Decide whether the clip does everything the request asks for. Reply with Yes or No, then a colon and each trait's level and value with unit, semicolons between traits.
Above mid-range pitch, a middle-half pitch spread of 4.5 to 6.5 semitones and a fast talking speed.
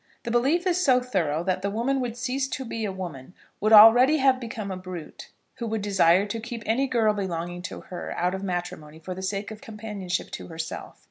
Yes: high, 210 Hz; average, 4.9 semitones; fast, 215 wpm